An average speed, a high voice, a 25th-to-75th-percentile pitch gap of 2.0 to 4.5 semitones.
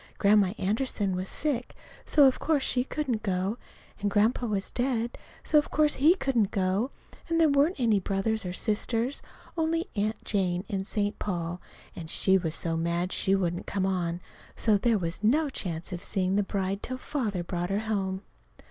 No: average, 180 wpm; high, 205 Hz; average, 5.0 semitones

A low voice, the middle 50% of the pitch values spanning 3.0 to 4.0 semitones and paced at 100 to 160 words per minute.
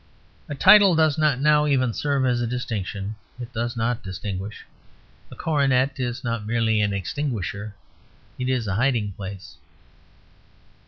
No: low, 120 Hz; average, 4.9 semitones; average, 145 wpm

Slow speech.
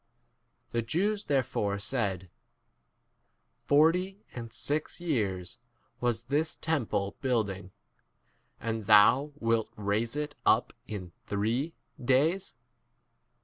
Yes: slow, 105 wpm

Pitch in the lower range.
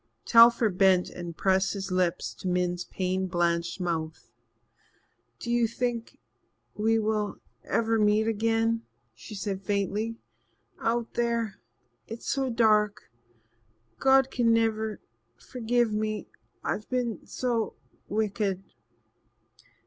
No: high, 215 Hz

